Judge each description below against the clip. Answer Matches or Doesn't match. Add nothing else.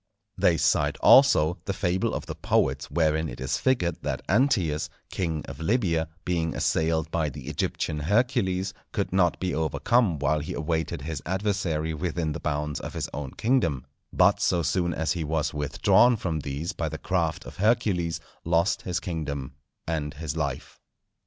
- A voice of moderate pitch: Doesn't match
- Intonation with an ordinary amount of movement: Matches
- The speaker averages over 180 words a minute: Doesn't match